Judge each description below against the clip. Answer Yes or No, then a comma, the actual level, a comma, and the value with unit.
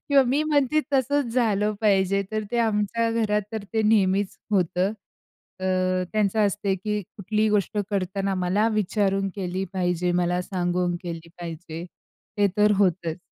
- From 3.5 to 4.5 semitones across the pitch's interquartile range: No, average, 2.9 semitones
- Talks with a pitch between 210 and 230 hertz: No, high, 200 Hz